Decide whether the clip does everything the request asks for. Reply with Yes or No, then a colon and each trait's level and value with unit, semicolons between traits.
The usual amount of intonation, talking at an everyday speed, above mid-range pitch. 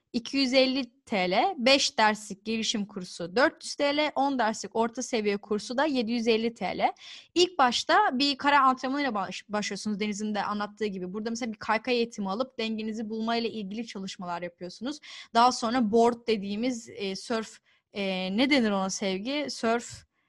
No: average, 4.1 semitones; fast, 145 wpm; high, 230 Hz